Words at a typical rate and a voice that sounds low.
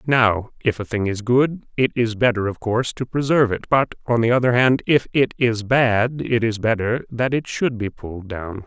No: fast, 220 wpm; low, 115 Hz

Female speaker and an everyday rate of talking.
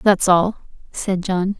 Yes: female; average, 150 wpm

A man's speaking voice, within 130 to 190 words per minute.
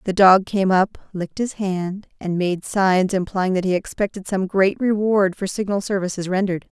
No: female; average, 185 wpm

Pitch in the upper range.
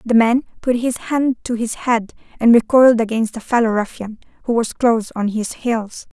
Yes: high, 230 Hz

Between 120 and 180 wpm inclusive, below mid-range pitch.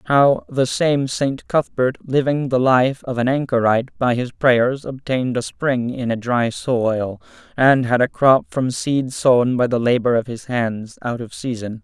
No: average, 190 wpm; low, 125 Hz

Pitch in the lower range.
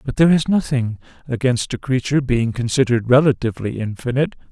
Yes: low, 125 Hz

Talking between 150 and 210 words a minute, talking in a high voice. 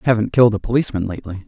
No: fast, 205 wpm; low, 110 Hz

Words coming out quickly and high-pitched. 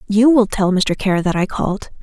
Yes: fast, 235 wpm; high, 205 Hz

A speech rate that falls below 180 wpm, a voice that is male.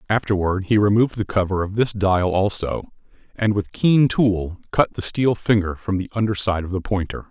No: average, 195 wpm; male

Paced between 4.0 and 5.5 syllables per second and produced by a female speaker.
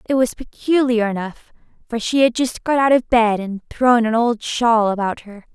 Yes: 4.6 syllables/s; female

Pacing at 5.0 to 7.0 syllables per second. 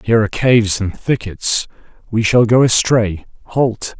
No: 4.7 syllables/s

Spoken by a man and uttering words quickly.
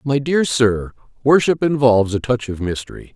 No: male; average, 170 wpm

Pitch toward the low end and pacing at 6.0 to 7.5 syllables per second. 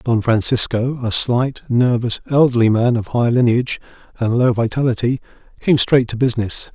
No: low, 120 Hz; 5.1 syllables/s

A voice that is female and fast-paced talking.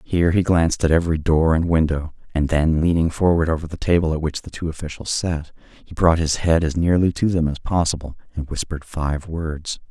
No: male; fast, 210 wpm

